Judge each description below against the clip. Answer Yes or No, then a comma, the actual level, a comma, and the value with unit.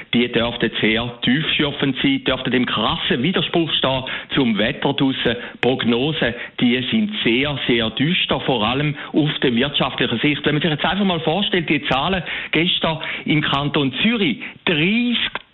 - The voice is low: No, medium, 150 Hz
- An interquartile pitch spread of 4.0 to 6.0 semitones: Yes, average, 4.9 semitones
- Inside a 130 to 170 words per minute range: Yes, average, 145 wpm